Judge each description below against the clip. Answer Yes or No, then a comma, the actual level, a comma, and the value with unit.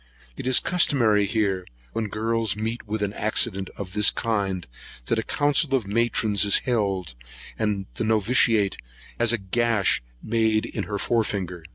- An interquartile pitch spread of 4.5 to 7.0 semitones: No, narrow, 2.6 semitones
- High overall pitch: No, low, 110 Hz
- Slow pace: No, average, 160 wpm